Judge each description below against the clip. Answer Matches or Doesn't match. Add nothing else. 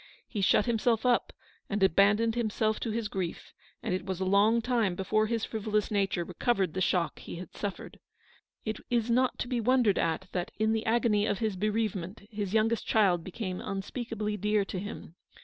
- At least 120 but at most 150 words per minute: Doesn't match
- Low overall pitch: Doesn't match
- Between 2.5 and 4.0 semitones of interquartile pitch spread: Matches